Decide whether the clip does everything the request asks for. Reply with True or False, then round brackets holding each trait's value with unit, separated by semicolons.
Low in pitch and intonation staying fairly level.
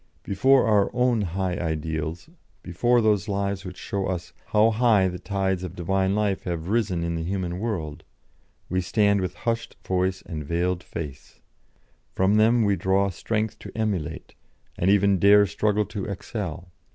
False (95 Hz; 3.0 semitones)